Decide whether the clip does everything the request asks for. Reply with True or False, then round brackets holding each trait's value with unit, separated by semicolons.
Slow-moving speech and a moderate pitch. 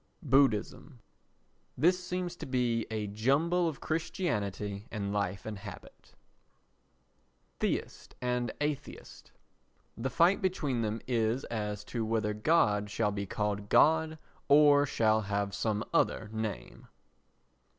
False (120 wpm; 115 Hz)